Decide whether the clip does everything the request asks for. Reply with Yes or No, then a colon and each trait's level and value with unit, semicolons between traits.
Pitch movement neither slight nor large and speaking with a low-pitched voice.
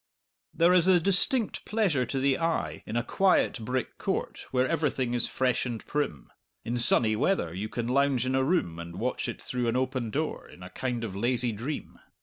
Yes: average, 4.4 semitones; low, 125 Hz